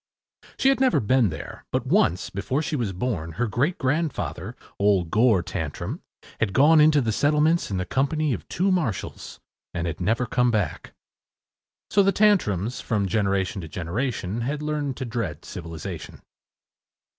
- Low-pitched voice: Yes, low, 115 Hz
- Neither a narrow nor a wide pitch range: No, wide, 7.9 semitones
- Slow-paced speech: No, average, 155 wpm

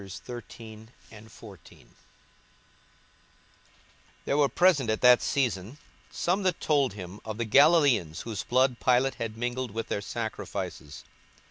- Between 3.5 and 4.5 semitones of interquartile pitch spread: Yes, average, 4.2 semitones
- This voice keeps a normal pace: No, slow, 115 wpm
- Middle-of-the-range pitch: No, low, 115 Hz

